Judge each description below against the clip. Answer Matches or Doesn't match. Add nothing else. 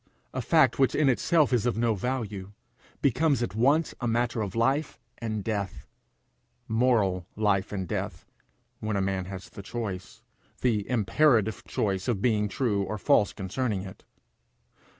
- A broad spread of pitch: Doesn't match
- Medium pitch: Doesn't match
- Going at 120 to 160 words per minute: Matches